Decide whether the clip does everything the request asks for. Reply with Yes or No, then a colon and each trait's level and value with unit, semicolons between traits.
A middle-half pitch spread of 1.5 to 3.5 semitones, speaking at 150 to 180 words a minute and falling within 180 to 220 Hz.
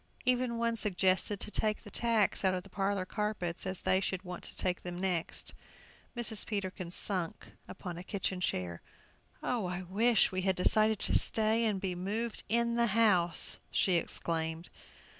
Yes: average, 3.2 semitones; average, 170 wpm; high, 190 Hz